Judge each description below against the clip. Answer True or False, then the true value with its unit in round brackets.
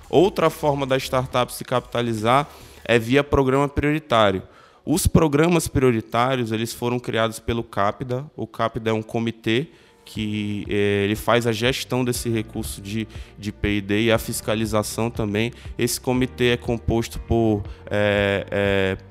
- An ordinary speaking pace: True (140 wpm)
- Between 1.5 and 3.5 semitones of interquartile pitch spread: True (3.0 semitones)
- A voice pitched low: True (115 Hz)